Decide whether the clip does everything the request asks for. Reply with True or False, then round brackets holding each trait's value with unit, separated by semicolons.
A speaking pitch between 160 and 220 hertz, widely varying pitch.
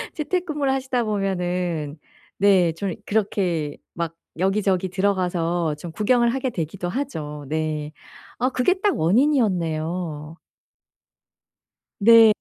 True (185 Hz; 6.1 semitones)